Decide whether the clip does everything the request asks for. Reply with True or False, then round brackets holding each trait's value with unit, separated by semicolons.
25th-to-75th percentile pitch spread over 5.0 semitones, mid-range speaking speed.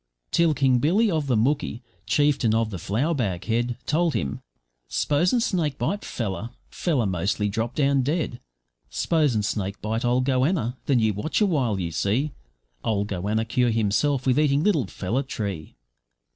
True (5.6 semitones; 160 wpm)